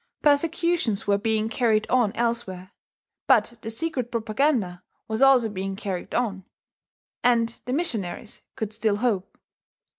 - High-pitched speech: Yes, high, 225 Hz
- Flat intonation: No, average, 3.5 semitones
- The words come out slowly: Yes, slow, 125 wpm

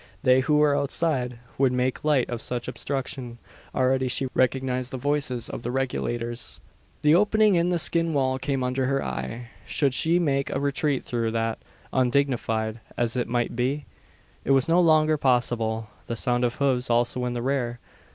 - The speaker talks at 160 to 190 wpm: Yes, average, 175 wpm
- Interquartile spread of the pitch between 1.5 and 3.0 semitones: Yes, average, 2.7 semitones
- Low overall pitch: Yes, low, 130 Hz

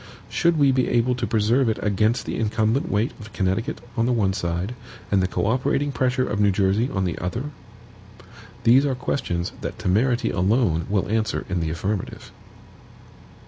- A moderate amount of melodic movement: Yes, average, 4.7 semitones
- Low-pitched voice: Yes, low, 110 Hz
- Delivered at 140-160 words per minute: No, average, 175 wpm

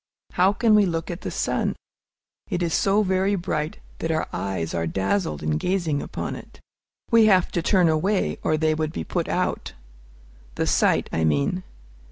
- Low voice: No, medium, 165 Hz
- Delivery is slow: No, average, 180 wpm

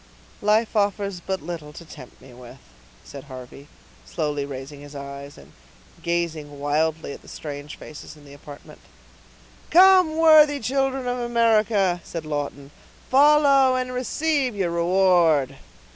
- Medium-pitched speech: Yes, medium, 170 Hz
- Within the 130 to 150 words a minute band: Yes, slow, 135 wpm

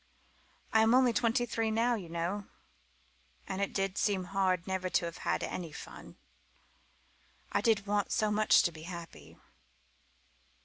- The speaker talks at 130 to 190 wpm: Yes, average, 150 wpm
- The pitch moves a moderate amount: Yes, average, 3.5 semitones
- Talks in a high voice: Yes, high, 195 Hz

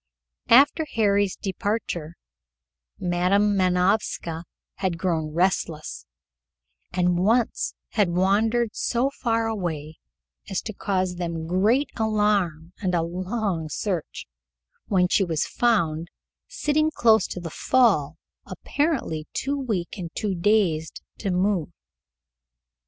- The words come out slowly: Yes, slow, 110 wpm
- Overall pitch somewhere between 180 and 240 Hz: Yes, high, 190 Hz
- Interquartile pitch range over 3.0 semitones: Yes, average, 4.3 semitones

